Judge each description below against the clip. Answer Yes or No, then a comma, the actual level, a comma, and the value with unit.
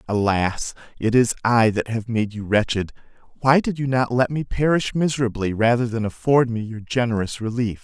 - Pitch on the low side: Yes, low, 115 Hz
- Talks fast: No, average, 185 wpm